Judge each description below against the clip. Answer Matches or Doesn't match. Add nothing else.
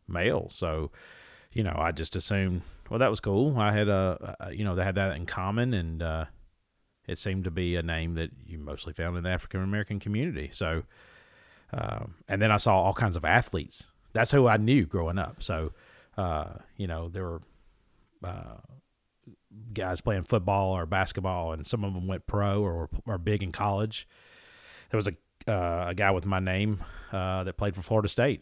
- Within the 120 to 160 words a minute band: Doesn't match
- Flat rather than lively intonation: Doesn't match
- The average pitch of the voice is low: Matches